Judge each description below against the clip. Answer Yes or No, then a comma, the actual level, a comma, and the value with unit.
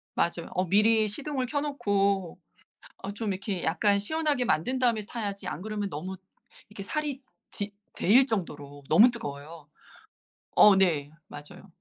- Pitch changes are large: No, average, 4.8 semitones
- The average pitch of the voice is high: Yes, high, 200 Hz